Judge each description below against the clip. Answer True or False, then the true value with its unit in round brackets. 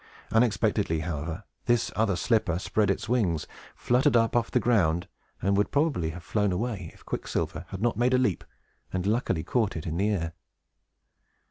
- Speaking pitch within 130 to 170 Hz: False (100 Hz)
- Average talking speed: True (170 wpm)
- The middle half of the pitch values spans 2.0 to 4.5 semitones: False (5.4 semitones)